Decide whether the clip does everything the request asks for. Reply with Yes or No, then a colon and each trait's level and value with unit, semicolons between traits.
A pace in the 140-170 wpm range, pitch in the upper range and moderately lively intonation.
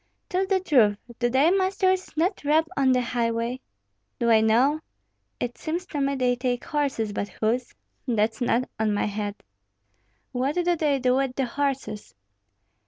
Yes: average, 165 wpm; very high, 255 Hz; average, 4.6 semitones